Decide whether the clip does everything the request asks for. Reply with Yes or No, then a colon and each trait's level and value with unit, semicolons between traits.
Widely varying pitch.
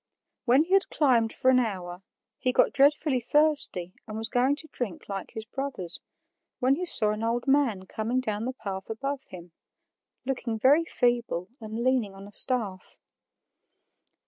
No: average, 4.3 semitones